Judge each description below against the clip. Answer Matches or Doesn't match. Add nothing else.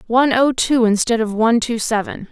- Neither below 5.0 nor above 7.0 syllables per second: Matches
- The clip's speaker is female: Matches